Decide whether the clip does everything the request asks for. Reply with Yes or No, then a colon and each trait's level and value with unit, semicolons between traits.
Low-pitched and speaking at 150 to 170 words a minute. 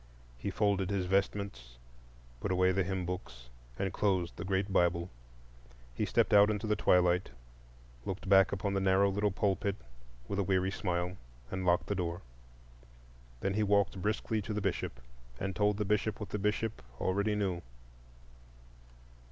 Yes: very low, 95 Hz; average, 160 wpm